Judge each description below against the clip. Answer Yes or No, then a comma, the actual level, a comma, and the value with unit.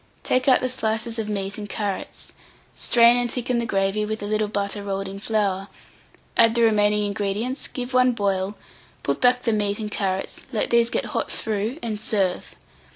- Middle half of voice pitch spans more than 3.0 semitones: No, average, 2.7 semitones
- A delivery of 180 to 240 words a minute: Yes, average, 185 wpm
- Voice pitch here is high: Yes, high, 215 Hz